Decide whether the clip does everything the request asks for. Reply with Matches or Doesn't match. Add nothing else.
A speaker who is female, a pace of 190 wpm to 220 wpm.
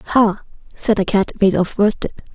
Doesn't match